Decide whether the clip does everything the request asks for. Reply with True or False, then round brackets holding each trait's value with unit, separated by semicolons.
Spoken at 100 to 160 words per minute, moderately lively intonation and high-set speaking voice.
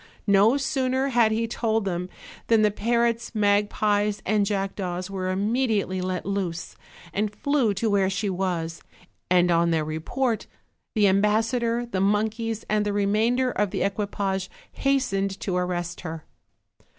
True (140 wpm; 3.2 semitones; 205 Hz)